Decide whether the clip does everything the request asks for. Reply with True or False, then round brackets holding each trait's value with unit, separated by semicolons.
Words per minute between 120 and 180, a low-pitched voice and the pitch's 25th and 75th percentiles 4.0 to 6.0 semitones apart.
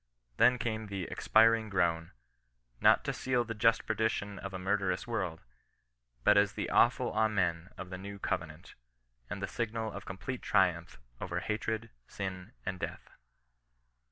False (155 wpm; 100 Hz; 3.4 semitones)